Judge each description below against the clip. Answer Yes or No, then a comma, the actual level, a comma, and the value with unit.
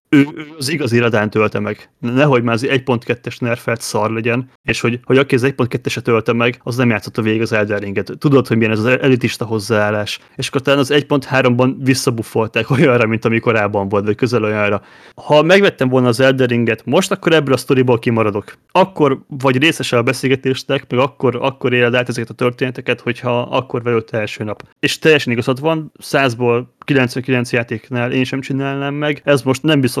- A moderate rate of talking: No, fast, 190 wpm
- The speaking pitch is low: Yes, low, 125 Hz